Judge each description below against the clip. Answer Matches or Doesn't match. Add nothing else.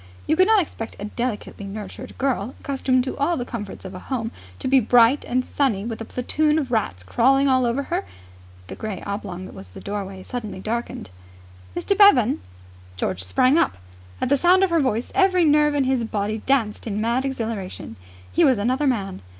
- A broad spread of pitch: Doesn't match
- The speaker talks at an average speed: Matches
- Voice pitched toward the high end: Matches